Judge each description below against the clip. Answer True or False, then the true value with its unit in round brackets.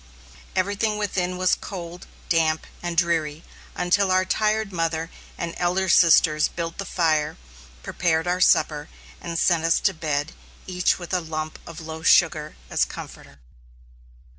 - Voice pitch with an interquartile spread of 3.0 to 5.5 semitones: False (2.4 semitones)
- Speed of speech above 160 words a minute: False (140 wpm)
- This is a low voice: False (170 Hz)